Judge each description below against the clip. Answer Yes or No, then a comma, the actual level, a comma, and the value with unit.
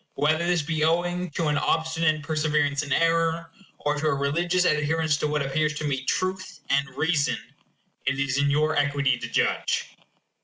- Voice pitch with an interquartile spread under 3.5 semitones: Yes, narrow, 2.4 semitones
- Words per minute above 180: No, average, 175 wpm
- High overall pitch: No, medium, 155 Hz